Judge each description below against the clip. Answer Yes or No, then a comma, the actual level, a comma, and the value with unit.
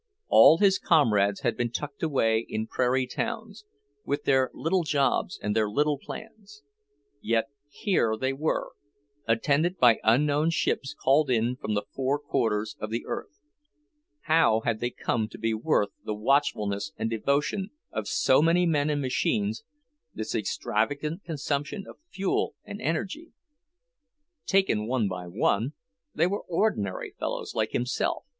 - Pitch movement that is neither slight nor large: No, wide, 6.2 semitones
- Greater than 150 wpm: No, average, 145 wpm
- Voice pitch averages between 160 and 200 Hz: No, low, 135 Hz